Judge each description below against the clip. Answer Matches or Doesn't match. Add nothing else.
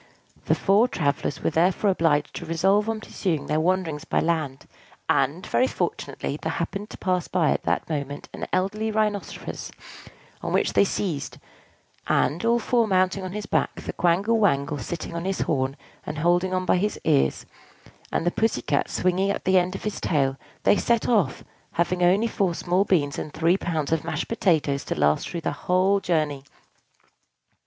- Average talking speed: Matches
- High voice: Doesn't match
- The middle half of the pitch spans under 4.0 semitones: Doesn't match